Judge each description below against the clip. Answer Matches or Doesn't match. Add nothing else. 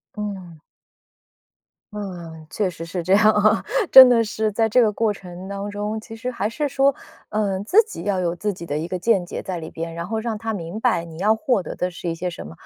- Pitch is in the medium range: Doesn't match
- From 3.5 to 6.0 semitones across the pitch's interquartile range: Matches